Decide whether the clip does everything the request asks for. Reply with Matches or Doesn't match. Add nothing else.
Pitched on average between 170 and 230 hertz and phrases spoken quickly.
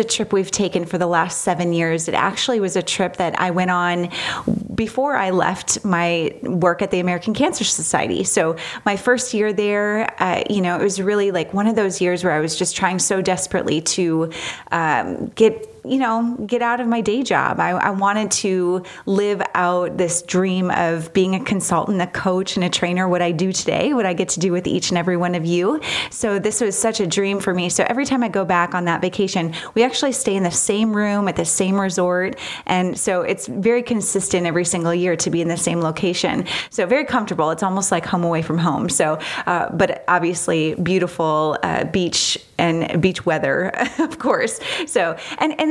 Matches